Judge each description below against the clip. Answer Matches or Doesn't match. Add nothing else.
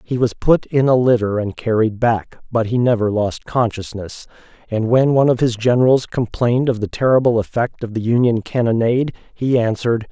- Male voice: Matches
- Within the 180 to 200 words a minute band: Matches